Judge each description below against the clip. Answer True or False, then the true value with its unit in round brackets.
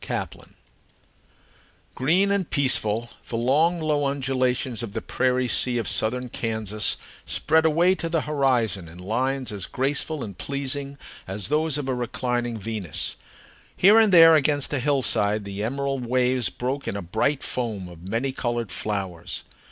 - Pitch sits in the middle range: False (125 Hz)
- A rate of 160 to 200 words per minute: False (150 wpm)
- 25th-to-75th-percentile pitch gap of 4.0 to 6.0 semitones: True (4.4 semitones)